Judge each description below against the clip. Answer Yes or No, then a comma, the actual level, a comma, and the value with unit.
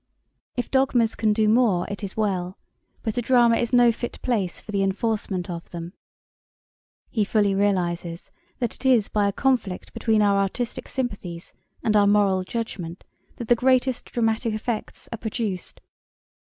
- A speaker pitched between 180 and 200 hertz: No, high, 215 Hz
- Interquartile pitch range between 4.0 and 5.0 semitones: No, average, 3.5 semitones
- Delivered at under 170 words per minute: Yes, average, 160 wpm